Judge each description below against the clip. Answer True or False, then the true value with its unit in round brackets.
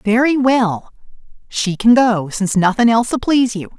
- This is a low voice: False (225 Hz)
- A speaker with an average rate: True (160 wpm)